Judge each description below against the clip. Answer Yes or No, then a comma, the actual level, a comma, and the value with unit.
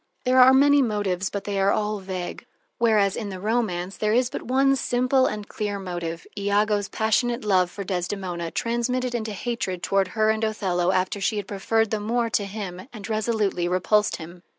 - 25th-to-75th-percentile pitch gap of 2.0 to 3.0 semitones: No, average, 3.4 semitones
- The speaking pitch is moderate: No, high, 210 Hz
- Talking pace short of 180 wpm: No, average, 185 wpm